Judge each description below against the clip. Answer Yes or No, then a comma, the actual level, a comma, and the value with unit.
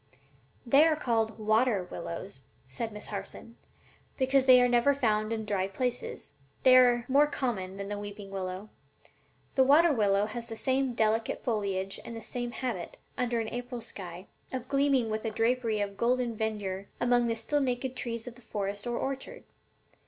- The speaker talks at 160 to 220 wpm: Yes, average, 175 wpm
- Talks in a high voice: Yes, high, 230 Hz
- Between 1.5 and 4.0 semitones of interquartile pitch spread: Yes, average, 3.4 semitones